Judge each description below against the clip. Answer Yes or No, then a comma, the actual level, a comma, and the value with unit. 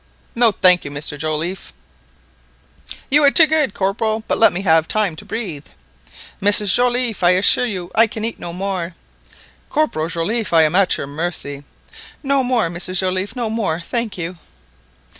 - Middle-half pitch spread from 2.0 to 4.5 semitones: No, average, 5.2 semitones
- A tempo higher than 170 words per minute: No, average, 165 wpm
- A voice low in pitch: No, high, 190 Hz